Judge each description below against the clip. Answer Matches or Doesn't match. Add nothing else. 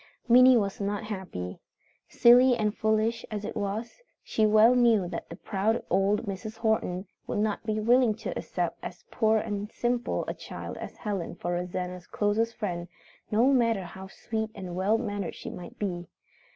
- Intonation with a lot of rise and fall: Doesn't match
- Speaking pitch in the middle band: Doesn't match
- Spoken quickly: Doesn't match